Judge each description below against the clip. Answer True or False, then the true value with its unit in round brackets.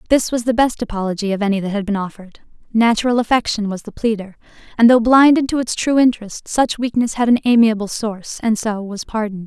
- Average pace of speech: False (210 wpm)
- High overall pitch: True (225 Hz)